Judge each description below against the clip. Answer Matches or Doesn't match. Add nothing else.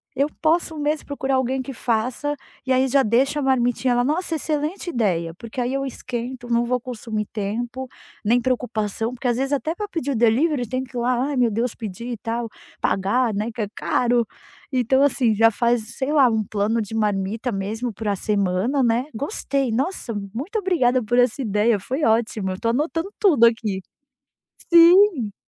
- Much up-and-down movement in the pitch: Doesn't match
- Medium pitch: Doesn't match